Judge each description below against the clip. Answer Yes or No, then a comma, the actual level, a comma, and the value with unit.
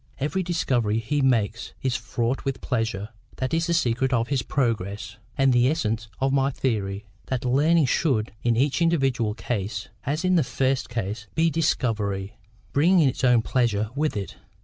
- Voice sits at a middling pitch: No, low, 125 Hz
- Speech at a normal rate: Yes, average, 160 wpm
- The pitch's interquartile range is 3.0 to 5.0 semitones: Yes, average, 4.1 semitones